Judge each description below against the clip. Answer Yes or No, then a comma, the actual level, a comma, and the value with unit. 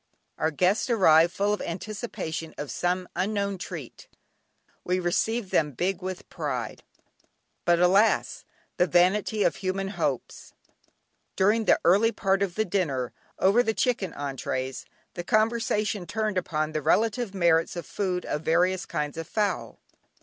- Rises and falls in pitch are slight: No, average, 4.0 semitones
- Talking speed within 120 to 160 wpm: Yes, average, 140 wpm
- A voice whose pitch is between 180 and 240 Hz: Yes, medium, 185 Hz